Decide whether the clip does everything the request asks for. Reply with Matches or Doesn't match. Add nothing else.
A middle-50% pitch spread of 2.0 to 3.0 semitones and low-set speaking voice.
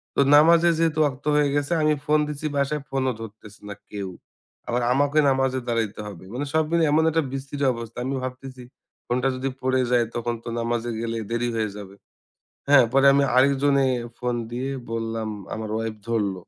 Doesn't match